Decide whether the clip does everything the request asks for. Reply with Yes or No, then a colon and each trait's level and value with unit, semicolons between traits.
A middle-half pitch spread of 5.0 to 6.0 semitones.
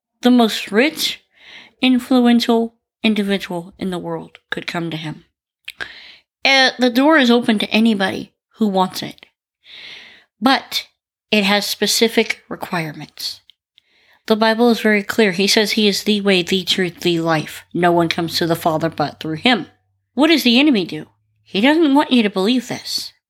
Yes: wide, 5.6 semitones